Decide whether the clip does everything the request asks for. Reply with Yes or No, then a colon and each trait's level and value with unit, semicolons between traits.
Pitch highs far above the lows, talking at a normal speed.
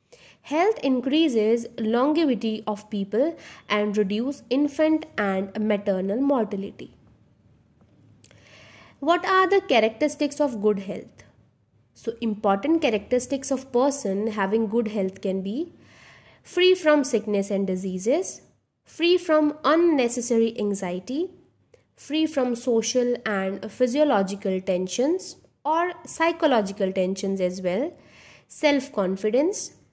No: wide, 6.8 semitones; slow, 100 wpm